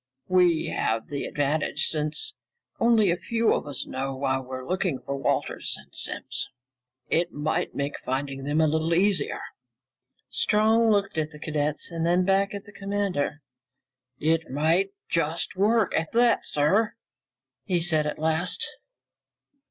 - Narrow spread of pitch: No, average, 5.1 semitones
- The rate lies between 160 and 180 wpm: No, average, 145 wpm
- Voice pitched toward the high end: No, medium, 165 Hz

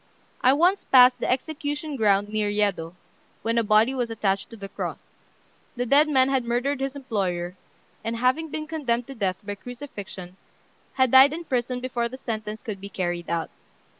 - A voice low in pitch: No, high, 235 Hz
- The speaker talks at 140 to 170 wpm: No, average, 180 wpm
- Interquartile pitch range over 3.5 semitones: Yes, average, 4.7 semitones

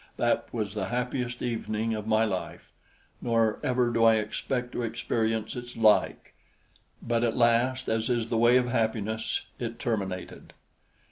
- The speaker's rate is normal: Yes, average, 150 wpm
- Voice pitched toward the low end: Yes, low, 115 Hz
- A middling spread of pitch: No, narrow, 1.7 semitones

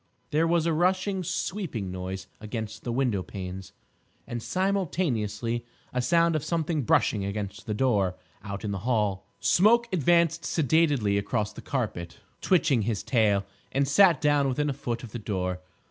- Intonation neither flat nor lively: No, wide, 8.0 semitones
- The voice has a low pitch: Yes, low, 120 Hz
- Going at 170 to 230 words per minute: No, average, 155 wpm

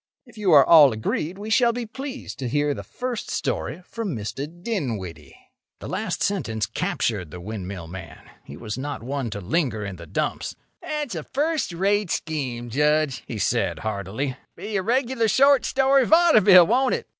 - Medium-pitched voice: Yes, medium, 155 Hz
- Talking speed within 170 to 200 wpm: Yes, average, 175 wpm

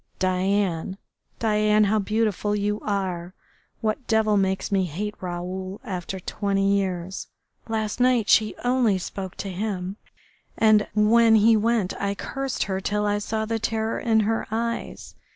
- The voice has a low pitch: No, high, 210 Hz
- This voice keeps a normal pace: Yes, average, 145 wpm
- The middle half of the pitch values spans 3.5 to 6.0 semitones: No, narrow, 2.5 semitones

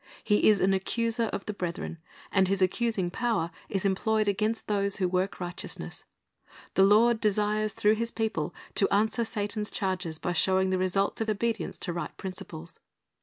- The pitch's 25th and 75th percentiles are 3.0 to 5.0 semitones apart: No, narrow, 2.6 semitones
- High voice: Yes, high, 200 Hz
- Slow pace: No, average, 170 wpm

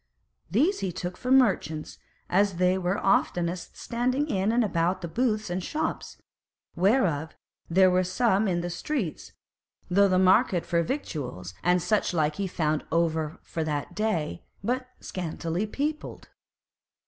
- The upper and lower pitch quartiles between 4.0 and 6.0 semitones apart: Yes, average, 4.4 semitones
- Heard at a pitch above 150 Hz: Yes, medium, 185 Hz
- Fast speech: No, average, 150 wpm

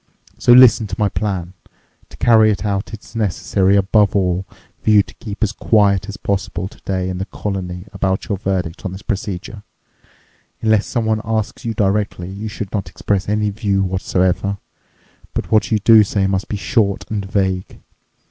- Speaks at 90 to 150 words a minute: No, average, 175 wpm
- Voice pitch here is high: No, low, 100 Hz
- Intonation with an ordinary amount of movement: No, narrow, 2.1 semitones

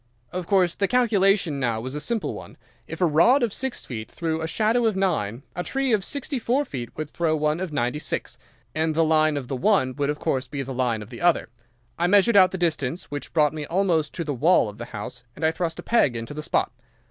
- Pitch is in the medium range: Yes, medium, 160 Hz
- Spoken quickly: Yes, fast, 245 wpm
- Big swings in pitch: Yes, wide, 5.7 semitones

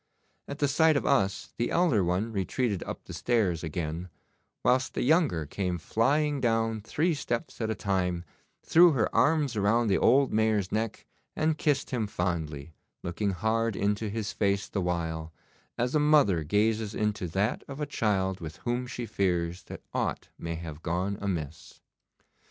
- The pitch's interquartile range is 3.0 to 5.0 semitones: No, wide, 5.5 semitones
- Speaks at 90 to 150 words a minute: No, average, 165 wpm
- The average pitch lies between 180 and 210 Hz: No, low, 105 Hz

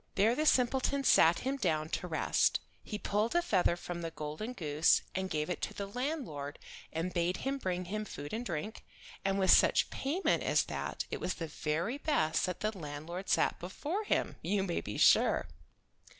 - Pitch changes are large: Yes, wide, 6.8 semitones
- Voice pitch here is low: No, high, 190 Hz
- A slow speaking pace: No, average, 190 wpm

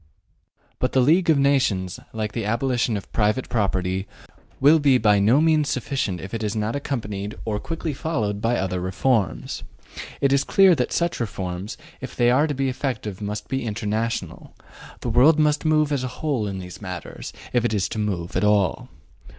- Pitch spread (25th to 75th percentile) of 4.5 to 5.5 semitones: Yes, average, 5.1 semitones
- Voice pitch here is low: Yes, low, 115 Hz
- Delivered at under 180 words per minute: No, average, 185 wpm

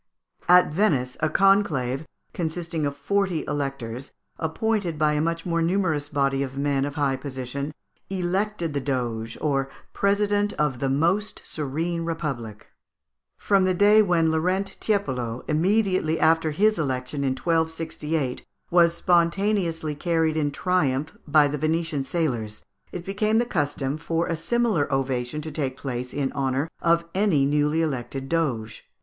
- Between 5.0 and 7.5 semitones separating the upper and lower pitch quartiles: No, average, 4.2 semitones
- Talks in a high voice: No, medium, 155 Hz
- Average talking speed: Yes, average, 145 wpm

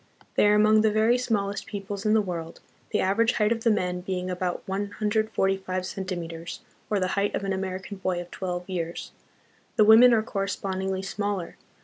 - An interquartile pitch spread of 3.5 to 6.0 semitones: No, narrow, 2.4 semitones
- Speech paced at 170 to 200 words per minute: Yes, average, 180 wpm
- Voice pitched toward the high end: Yes, high, 195 Hz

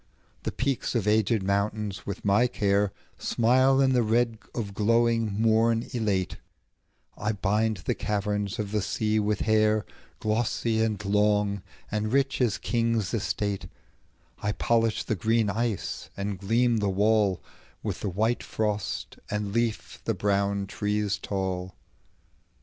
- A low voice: Yes, low, 105 Hz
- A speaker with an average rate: No, slow, 125 wpm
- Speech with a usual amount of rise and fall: No, narrow, 2.1 semitones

